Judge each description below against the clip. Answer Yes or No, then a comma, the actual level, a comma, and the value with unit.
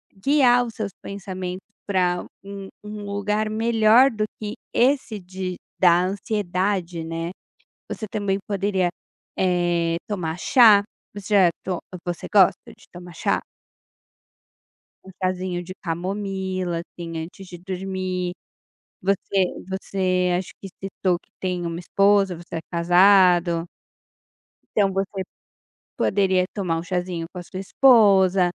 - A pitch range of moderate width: No, narrow, 2.3 semitones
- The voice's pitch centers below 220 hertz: Yes, high, 190 Hz